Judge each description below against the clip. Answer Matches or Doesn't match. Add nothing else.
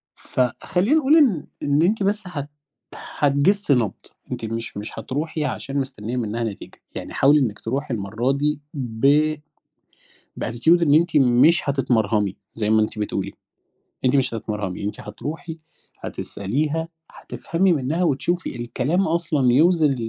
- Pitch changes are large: Matches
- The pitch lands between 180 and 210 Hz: Doesn't match